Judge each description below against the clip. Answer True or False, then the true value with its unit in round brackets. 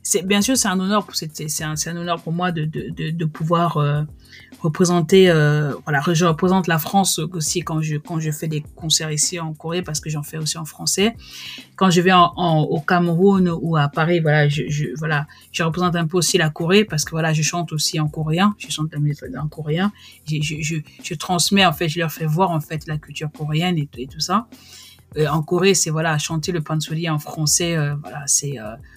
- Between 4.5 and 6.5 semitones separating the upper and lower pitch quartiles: False (2.5 semitones)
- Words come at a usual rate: False (235 wpm)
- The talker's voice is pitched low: False (160 Hz)